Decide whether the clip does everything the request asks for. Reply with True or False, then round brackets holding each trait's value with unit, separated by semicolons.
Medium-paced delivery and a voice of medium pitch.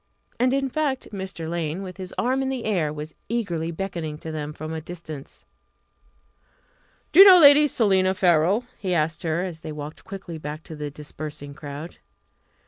True (175 wpm; 170 Hz)